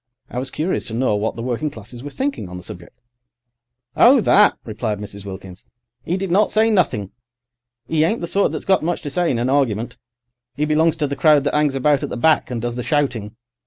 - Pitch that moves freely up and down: Yes, wide, 6.3 semitones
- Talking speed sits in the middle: No, fast, 225 wpm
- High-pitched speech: No, medium, 140 Hz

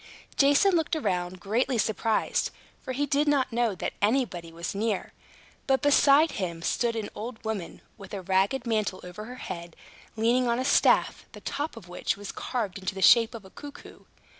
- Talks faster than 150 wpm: Yes, average, 185 wpm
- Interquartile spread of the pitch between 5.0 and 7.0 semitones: Yes, wide, 5.4 semitones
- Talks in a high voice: Yes, high, 225 Hz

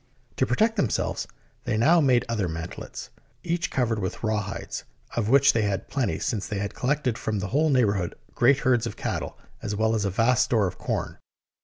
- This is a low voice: Yes, low, 115 Hz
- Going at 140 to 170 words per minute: No, average, 190 wpm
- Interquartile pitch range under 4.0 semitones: No, average, 4.3 semitones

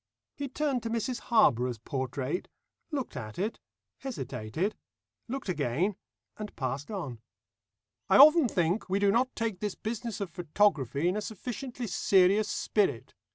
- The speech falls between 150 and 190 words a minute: No, average, 140 wpm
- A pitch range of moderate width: No, wide, 8.1 semitones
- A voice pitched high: Yes, high, 200 Hz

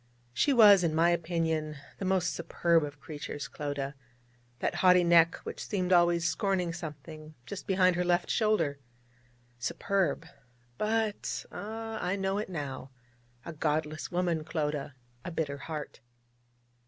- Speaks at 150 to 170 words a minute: No, slow, 135 wpm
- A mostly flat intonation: No, average, 3.5 semitones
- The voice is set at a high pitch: No, medium, 170 Hz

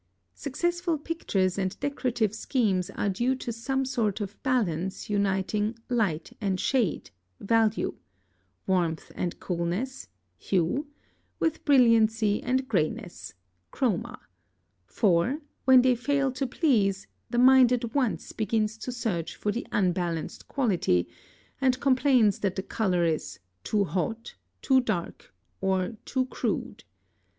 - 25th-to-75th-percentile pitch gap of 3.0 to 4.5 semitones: No, average, 5.3 semitones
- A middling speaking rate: No, slow, 125 wpm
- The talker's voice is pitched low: No, high, 220 Hz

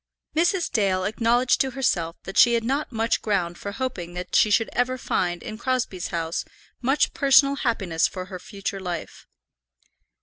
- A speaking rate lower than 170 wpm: No, average, 175 wpm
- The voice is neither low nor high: No, high, 220 Hz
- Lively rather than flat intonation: Yes, wide, 5.9 semitones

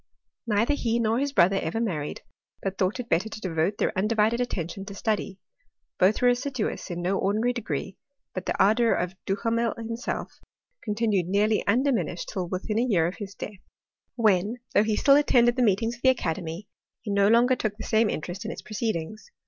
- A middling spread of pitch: Yes, average, 3.6 semitones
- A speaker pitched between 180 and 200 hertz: No, high, 215 Hz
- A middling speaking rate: Yes, average, 190 wpm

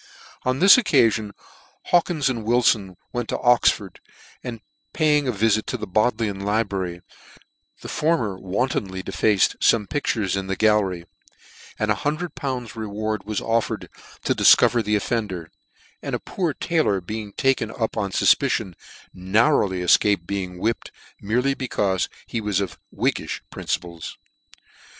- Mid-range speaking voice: No, low, 110 Hz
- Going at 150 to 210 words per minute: No, slow, 135 wpm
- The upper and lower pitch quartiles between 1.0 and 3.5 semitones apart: No, average, 4.1 semitones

